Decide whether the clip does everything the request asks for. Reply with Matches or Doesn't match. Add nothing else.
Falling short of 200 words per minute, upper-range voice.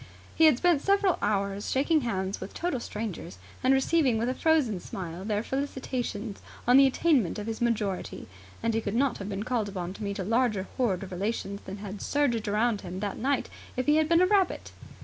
Doesn't match